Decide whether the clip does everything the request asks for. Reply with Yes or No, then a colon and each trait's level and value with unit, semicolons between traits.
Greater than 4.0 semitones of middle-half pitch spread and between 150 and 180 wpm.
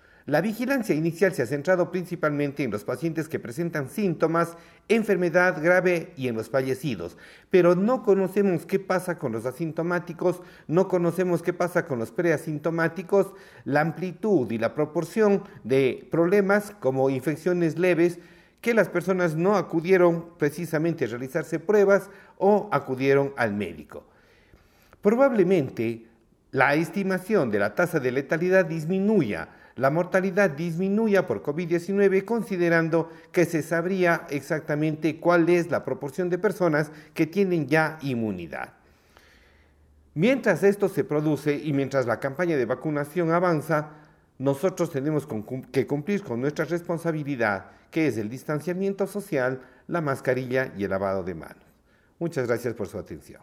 No: average, 4.8 semitones; average, 135 wpm